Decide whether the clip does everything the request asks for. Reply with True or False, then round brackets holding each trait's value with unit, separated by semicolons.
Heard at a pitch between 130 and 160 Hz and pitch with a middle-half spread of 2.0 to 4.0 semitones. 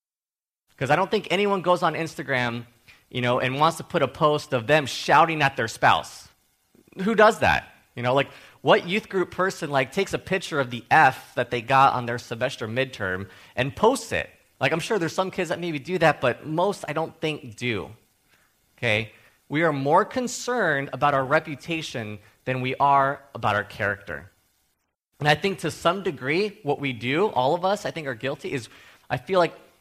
False (140 Hz; 5.6 semitones)